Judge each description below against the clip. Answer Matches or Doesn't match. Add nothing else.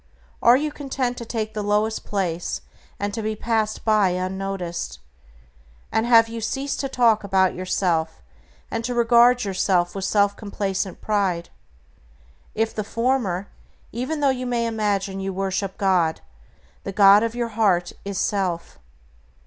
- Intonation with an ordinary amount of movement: Matches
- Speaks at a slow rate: Doesn't match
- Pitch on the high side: Matches